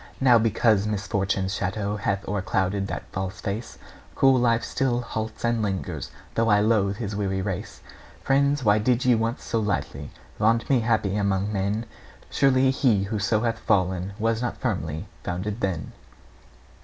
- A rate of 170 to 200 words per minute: No, average, 155 wpm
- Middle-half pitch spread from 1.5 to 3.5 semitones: Yes, average, 3.0 semitones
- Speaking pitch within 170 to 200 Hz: No, low, 105 Hz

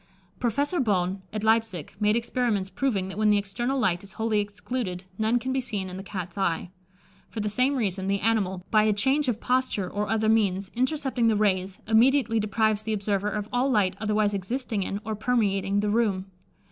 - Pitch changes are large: No, average, 3.2 semitones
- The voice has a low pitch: No, high, 210 Hz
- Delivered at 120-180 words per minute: No, average, 195 wpm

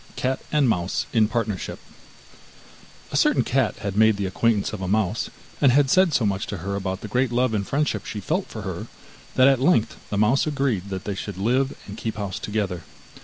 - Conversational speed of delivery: No, fast, 210 wpm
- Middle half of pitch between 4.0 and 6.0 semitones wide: Yes, average, 4.5 semitones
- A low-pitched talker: Yes, low, 110 Hz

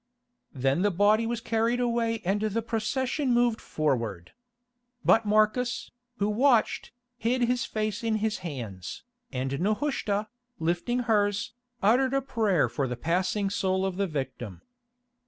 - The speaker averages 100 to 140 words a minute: Yes, slow, 135 wpm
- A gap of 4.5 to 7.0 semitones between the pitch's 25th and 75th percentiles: Yes, average, 5.2 semitones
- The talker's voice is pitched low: No, high, 210 Hz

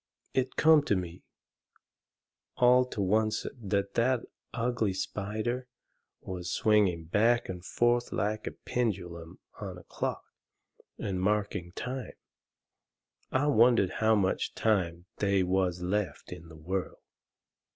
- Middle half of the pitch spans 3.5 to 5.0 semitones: Yes, average, 4.6 semitones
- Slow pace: Yes, slow, 120 wpm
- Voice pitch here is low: Yes, low, 105 Hz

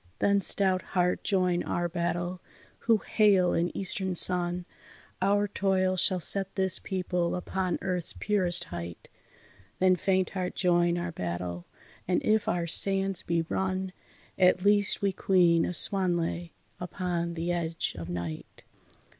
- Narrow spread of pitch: Yes, narrow, 1.8 semitones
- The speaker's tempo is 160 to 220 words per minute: No, average, 140 wpm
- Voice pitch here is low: No, medium, 180 Hz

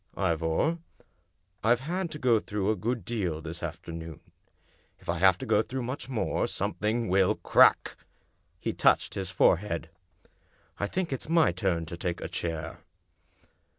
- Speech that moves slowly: No, average, 160 wpm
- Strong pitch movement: Yes, wide, 6.2 semitones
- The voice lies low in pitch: Yes, very low, 95 Hz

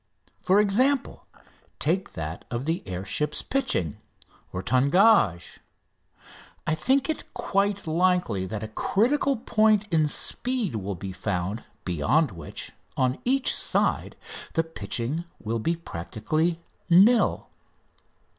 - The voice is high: No, medium, 160 Hz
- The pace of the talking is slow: Yes, slow, 115 wpm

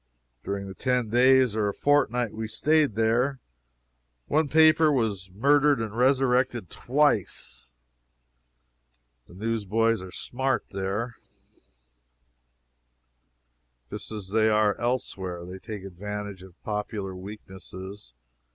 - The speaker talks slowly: Yes, slow, 105 wpm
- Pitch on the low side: Yes, low, 110 Hz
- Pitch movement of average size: Yes, average, 4.5 semitones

